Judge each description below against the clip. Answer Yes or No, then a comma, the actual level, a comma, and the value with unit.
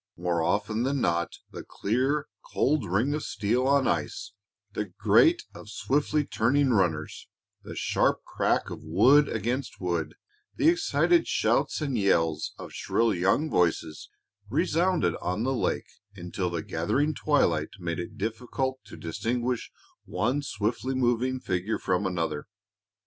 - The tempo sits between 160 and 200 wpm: No, average, 140 wpm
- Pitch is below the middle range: Yes, low, 115 Hz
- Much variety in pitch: Yes, wide, 7.6 semitones